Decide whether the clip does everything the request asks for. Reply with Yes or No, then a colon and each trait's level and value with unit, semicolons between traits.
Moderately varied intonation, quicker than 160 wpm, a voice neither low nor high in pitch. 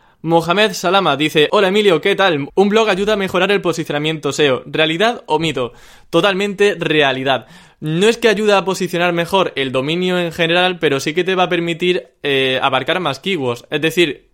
Yes: average, 3.9 semitones; average, 185 wpm; medium, 175 Hz